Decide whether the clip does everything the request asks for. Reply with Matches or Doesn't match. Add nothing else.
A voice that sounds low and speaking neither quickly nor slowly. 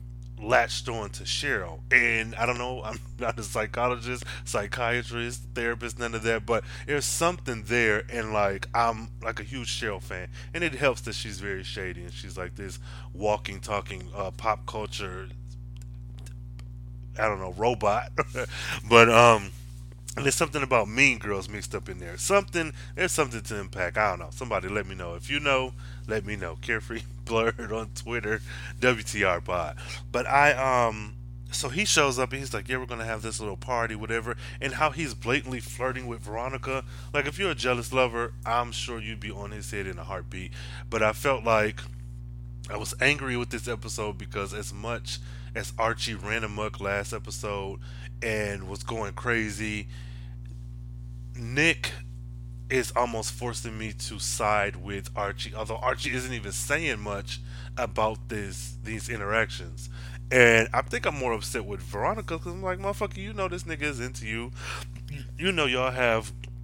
Matches